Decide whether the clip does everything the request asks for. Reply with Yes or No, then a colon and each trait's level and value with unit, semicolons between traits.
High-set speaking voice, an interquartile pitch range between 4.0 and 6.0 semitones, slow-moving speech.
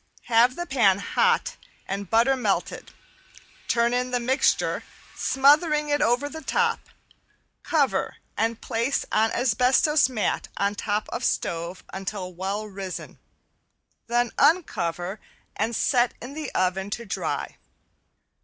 Yes: high, 235 Hz; average, 5.2 semitones; slow, 125 wpm